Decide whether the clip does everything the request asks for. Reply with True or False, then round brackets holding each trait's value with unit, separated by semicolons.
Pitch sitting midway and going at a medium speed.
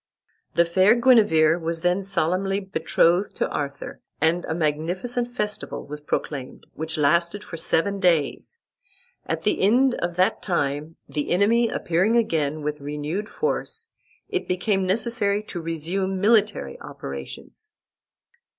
False (180 Hz; 125 wpm)